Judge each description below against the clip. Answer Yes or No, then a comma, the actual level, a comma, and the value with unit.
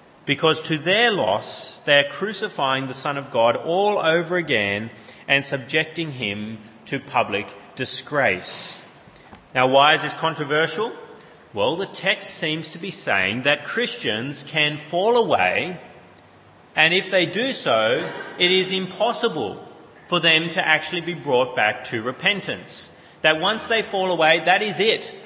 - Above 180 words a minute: No, average, 145 wpm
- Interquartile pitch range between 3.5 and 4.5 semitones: No, average, 5.2 semitones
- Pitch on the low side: No, medium, 160 Hz